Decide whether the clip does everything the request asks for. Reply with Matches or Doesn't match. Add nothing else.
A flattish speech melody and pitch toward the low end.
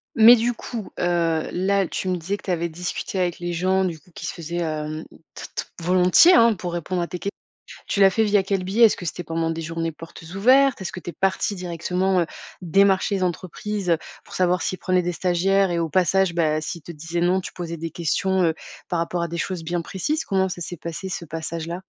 Doesn't match